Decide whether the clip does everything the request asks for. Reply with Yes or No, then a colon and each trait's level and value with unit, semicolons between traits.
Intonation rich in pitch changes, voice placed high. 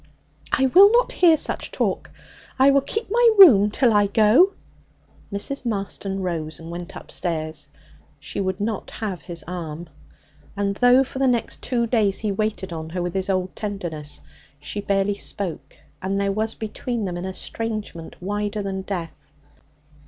No: average, 4.1 semitones; high, 200 Hz